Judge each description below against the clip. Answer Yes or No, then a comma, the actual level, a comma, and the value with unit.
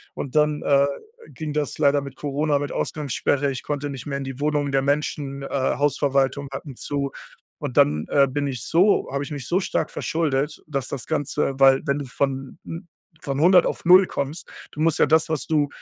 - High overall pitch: No, medium, 140 Hz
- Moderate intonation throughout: No, narrow, 1.7 semitones